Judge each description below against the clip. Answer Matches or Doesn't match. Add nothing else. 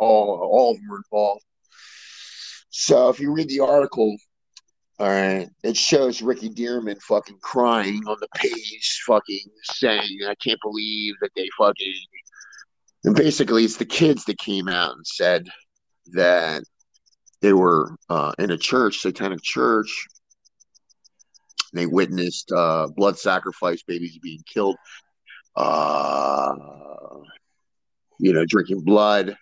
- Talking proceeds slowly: Matches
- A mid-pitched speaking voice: Doesn't match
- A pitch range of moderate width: Matches